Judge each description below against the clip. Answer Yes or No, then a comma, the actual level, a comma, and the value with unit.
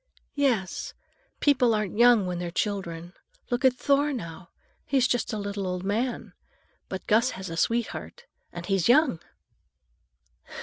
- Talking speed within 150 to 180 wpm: No, average, 140 wpm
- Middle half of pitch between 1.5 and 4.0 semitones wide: No, wide, 5.4 semitones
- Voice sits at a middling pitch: No, high, 210 Hz